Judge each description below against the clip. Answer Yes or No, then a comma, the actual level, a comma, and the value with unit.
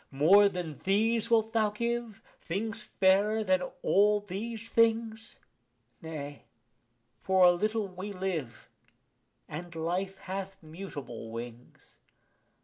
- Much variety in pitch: No, average, 3.8 semitones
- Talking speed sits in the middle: No, slow, 110 wpm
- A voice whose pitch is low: No, high, 195 Hz